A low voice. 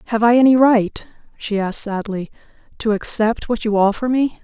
No: high, 220 Hz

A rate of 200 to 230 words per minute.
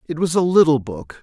No: fast, 245 wpm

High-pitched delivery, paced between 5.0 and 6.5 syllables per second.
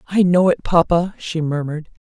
No: medium, 170 Hz; 5.1 syllables/s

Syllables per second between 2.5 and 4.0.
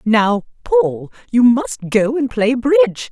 Yes: 3.5 syllables/s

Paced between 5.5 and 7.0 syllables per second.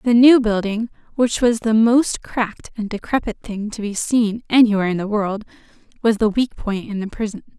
No: 5.1 syllables/s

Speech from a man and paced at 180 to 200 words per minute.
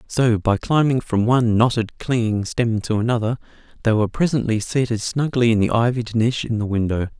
Yes: male; average, 185 wpm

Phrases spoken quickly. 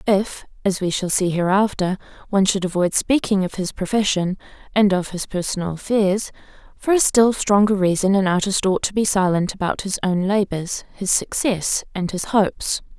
No: average, 175 wpm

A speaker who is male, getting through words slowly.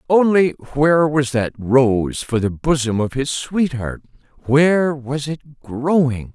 Yes: male; slow, 130 wpm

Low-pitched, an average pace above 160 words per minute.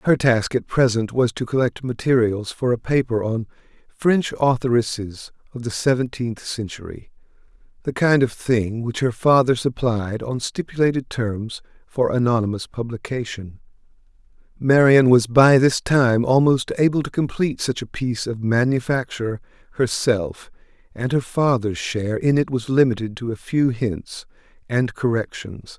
No: low, 120 Hz; average, 140 wpm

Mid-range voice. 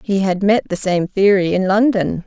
No: high, 195 Hz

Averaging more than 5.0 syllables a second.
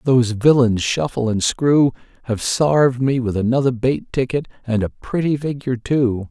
No: 4.9 syllables/s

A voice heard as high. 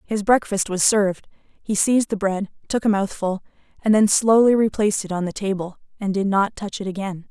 Yes: high, 200 Hz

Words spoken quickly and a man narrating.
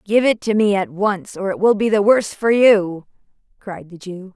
No: fast, 235 wpm; female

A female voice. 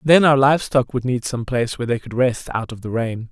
No: male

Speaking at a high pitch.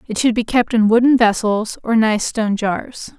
Yes: high, 225 Hz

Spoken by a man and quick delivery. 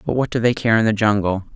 Yes: male; fast, 310 wpm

